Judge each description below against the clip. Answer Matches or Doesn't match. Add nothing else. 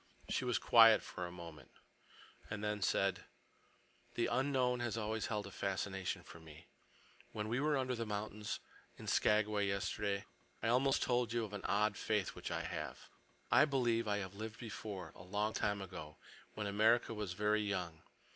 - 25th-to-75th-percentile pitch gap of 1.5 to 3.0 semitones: Matches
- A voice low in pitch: Matches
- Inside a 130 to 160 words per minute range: Doesn't match